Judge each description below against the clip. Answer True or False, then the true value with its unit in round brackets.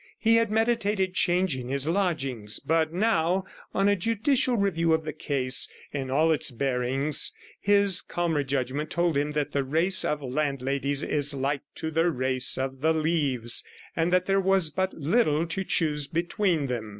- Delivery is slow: False (165 wpm)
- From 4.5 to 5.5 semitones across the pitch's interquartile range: True (5.2 semitones)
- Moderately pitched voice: True (160 Hz)